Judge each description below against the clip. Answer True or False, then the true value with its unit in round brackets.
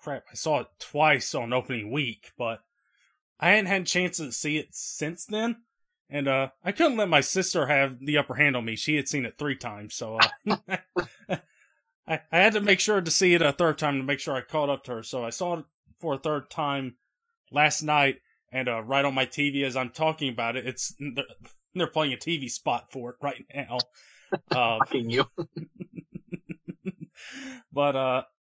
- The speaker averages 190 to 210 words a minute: True (205 wpm)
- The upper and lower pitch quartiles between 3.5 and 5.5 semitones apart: True (4.3 semitones)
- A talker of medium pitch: True (145 Hz)